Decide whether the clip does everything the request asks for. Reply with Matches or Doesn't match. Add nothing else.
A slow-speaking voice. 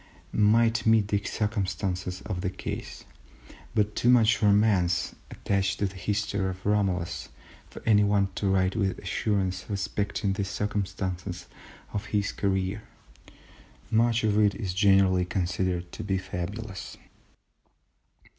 Matches